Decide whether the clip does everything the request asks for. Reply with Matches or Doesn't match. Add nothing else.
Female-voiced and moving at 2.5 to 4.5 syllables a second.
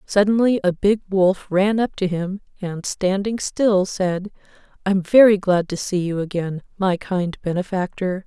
Matches